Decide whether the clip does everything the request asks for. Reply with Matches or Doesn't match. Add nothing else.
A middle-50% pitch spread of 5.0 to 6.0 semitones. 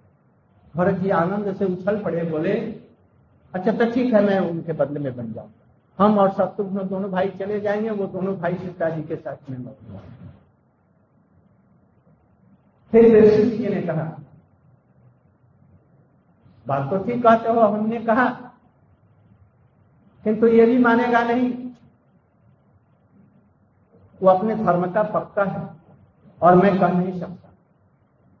Matches